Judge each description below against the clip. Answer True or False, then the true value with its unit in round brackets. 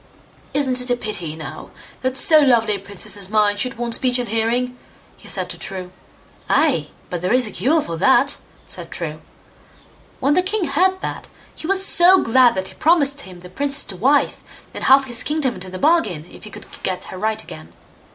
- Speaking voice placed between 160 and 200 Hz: False (245 Hz)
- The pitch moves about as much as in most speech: False (6.3 semitones)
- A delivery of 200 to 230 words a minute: True (205 wpm)